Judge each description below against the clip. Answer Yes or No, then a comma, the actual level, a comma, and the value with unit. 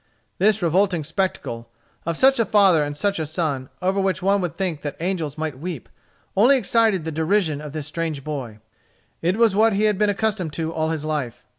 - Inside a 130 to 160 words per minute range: No, average, 200 wpm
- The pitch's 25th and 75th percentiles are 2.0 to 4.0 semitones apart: No, average, 4.6 semitones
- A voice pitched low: No, medium, 170 Hz